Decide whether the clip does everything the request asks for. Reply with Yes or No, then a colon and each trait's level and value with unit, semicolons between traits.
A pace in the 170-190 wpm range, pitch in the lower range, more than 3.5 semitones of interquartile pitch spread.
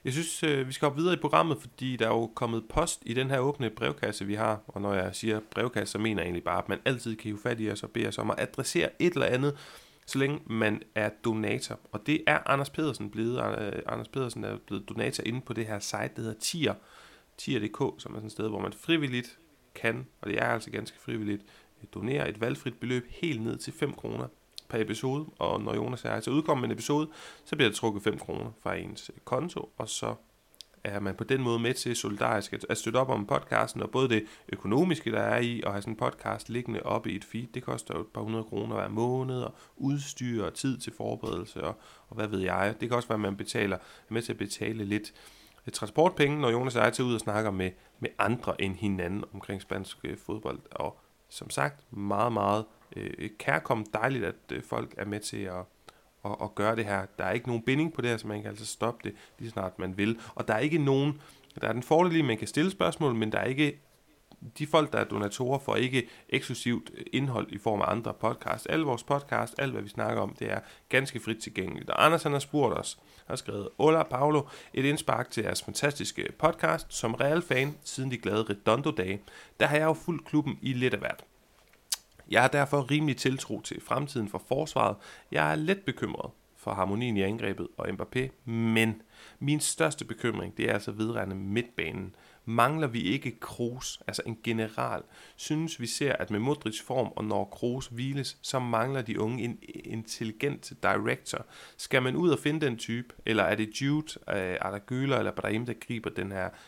No: average, 220 wpm; low, 115 Hz; average, 4.1 semitones